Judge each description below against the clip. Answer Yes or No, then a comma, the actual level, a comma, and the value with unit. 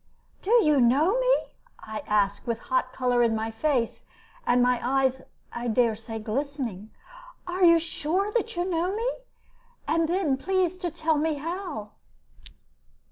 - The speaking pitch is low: No, very high, 285 Hz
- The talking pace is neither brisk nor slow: Yes, average, 150 wpm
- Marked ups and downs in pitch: Yes, wide, 6.8 semitones